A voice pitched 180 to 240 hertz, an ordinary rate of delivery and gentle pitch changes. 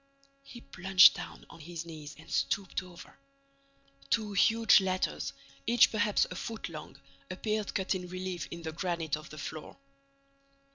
No: medium, 185 Hz; average, 150 wpm; average, 3.4 semitones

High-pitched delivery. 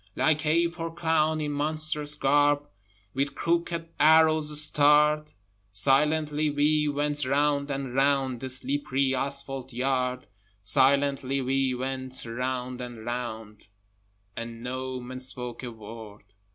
No: medium, 140 Hz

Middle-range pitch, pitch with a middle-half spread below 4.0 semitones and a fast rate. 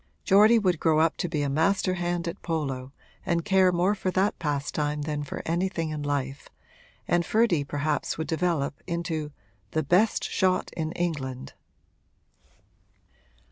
No: medium, 165 Hz; average, 3.6 semitones; average, 145 wpm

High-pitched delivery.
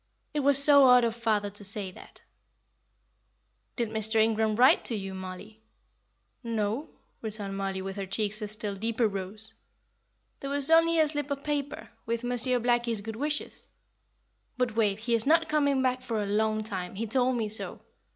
Yes: high, 225 Hz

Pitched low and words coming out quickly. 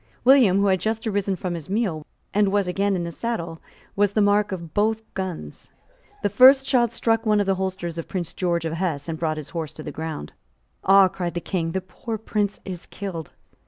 No: high, 190 Hz; fast, 215 wpm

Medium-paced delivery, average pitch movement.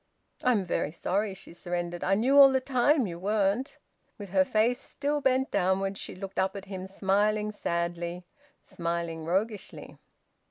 Yes: average, 155 wpm; average, 4.1 semitones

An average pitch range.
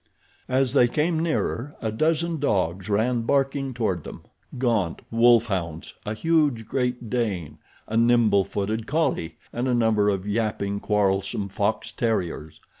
Yes: average, 4.1 semitones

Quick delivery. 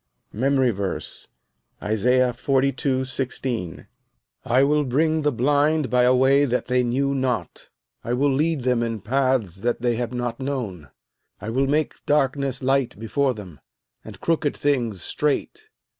No: average, 145 wpm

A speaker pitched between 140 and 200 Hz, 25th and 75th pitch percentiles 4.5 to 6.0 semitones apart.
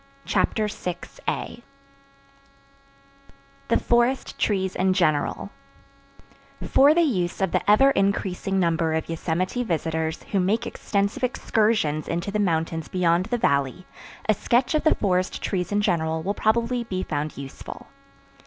Yes: high, 190 Hz; average, 4.9 semitones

